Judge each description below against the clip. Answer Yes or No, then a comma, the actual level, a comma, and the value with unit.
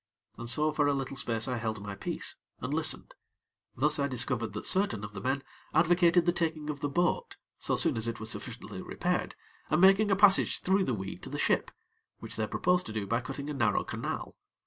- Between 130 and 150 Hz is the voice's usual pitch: Yes, medium, 140 Hz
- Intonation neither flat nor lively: No, wide, 7.1 semitones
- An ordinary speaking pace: No, fast, 215 wpm